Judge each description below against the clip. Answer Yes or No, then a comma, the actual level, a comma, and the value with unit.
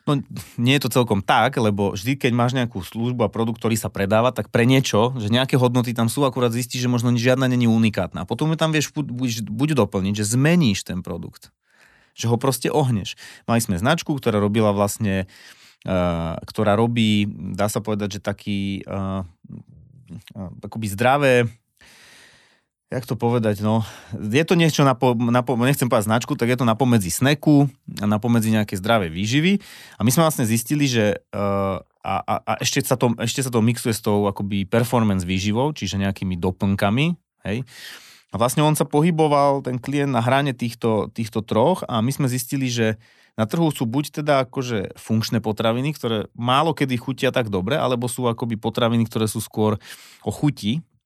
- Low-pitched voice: Yes, low, 115 Hz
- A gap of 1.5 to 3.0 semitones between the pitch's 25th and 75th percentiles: No, average, 3.8 semitones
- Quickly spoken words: Yes, fast, 180 wpm